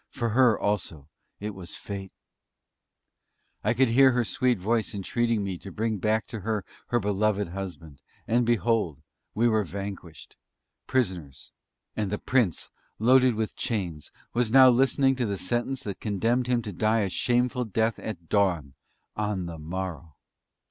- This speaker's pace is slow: No, average, 155 wpm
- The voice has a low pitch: Yes, low, 105 Hz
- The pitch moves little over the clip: No, average, 4.1 semitones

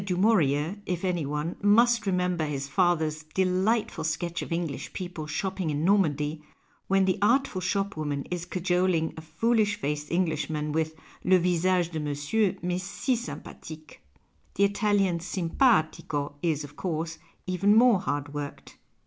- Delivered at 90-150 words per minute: Yes, average, 145 wpm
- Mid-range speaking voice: Yes, medium, 175 Hz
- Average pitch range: Yes, average, 3.9 semitones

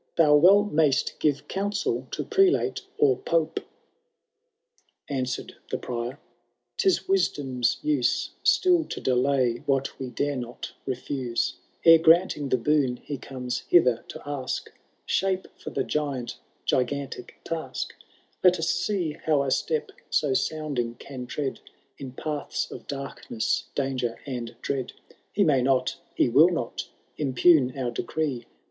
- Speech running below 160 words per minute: Yes, average, 140 wpm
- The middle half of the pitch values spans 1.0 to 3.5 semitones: No, average, 4.1 semitones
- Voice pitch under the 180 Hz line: Yes, medium, 140 Hz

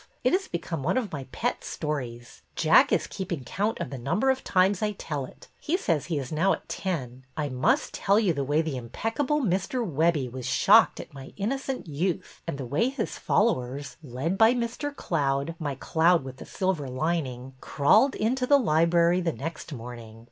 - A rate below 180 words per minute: No, average, 200 wpm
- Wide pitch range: Yes, wide, 7.0 semitones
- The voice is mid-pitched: Yes, medium, 165 Hz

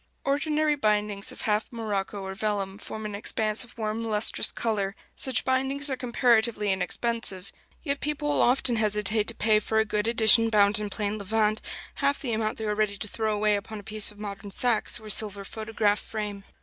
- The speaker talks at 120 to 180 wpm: No, average, 195 wpm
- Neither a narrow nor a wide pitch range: No, narrow, 1.9 semitones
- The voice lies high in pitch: Yes, high, 215 Hz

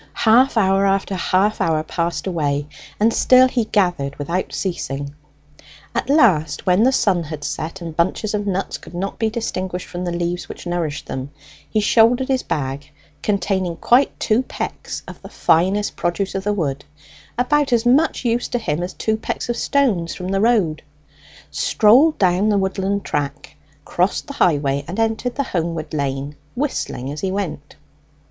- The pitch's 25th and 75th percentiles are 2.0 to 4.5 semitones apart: No, wide, 5.5 semitones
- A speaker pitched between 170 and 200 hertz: Yes, high, 190 Hz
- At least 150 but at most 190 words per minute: Yes, average, 170 wpm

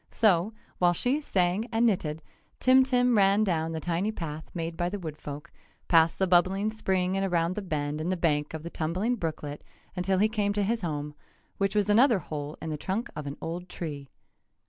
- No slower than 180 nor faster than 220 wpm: Yes, average, 200 wpm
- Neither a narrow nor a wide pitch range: Yes, average, 4.5 semitones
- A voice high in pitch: No, medium, 180 Hz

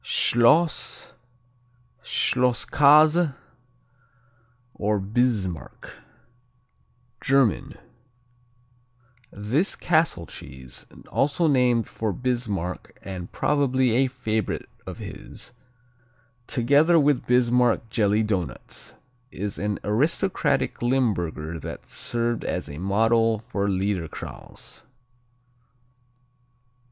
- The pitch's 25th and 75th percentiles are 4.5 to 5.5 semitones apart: Yes, average, 4.9 semitones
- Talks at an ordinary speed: No, slow, 75 wpm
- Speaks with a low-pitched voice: Yes, low, 120 Hz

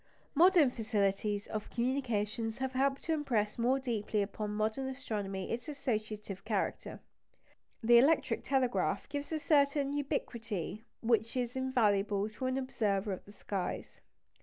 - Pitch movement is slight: No, average, 4.2 semitones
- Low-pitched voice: No, high, 235 Hz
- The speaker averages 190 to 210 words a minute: No, slow, 135 wpm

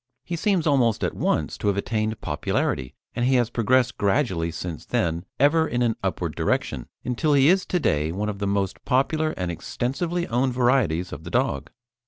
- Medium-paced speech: Yes, average, 190 wpm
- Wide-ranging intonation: Yes, wide, 6.1 semitones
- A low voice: Yes, low, 120 Hz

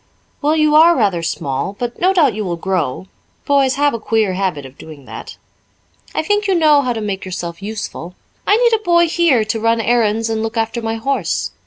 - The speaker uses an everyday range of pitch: No, wide, 7.5 semitones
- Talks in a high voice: Yes, high, 225 Hz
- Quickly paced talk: Yes, fast, 210 wpm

